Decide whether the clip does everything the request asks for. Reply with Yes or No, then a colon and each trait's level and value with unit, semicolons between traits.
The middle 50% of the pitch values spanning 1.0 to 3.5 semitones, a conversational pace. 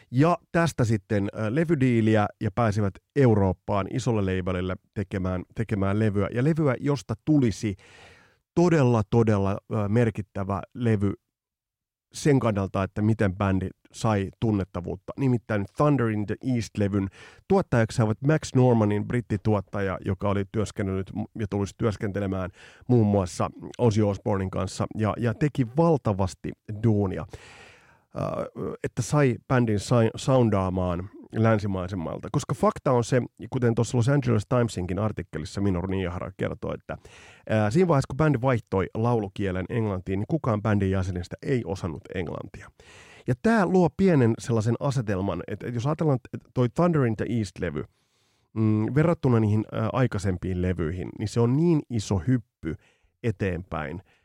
No: average, 4.2 semitones; average, 120 wpm